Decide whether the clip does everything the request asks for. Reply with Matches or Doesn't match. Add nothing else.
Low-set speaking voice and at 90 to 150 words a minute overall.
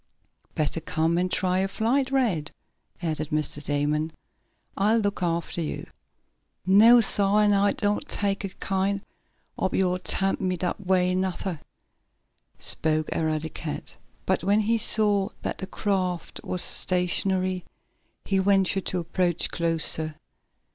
Doesn't match